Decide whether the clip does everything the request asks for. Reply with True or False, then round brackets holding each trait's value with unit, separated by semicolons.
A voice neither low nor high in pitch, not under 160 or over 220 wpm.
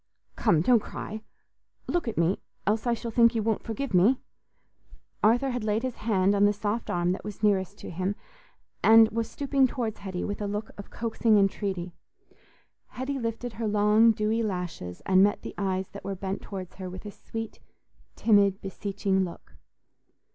False (210 Hz; 175 wpm)